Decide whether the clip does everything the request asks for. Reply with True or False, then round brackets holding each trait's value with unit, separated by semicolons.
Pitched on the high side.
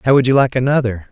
False (125 Hz)